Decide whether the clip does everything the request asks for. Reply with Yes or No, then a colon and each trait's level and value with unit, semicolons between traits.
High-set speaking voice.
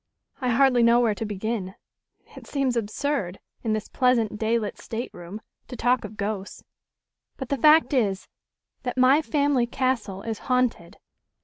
Yes: high, 235 Hz